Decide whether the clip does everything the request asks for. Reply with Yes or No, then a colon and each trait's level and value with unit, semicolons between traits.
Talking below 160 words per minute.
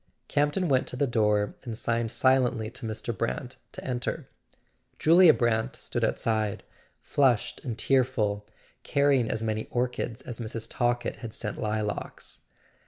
Yes: average, 140 wpm